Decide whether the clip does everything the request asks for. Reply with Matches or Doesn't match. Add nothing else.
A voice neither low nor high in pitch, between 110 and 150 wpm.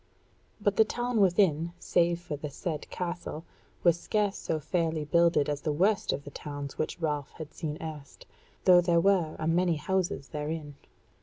Doesn't match